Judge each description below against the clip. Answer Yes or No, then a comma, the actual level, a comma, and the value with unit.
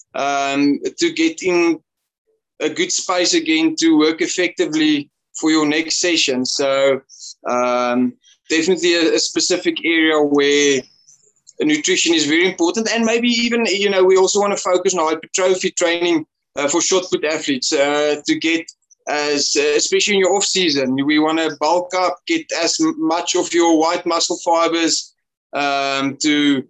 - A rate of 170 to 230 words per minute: No, average, 155 wpm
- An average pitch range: No, wide, 7.9 semitones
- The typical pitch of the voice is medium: Yes, medium, 170 Hz